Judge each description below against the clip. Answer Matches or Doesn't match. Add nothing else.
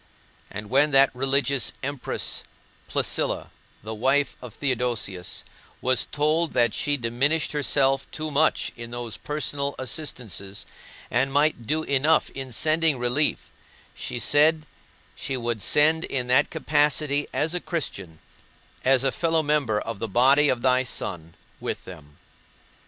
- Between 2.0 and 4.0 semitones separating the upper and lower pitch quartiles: Matches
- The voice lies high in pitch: Doesn't match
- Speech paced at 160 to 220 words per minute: Doesn't match